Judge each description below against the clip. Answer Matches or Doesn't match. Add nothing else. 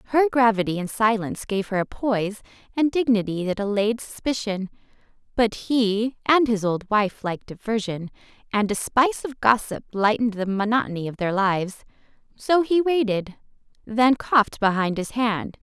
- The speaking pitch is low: Doesn't match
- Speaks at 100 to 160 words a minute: Matches